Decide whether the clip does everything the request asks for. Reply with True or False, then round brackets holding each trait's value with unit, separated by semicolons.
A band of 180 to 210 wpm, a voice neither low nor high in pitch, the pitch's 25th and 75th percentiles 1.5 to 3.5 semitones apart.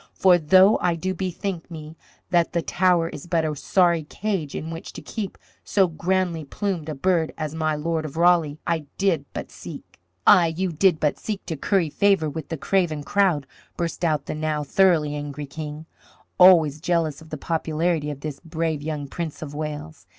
True (190 wpm; 160 Hz; 2.9 semitones)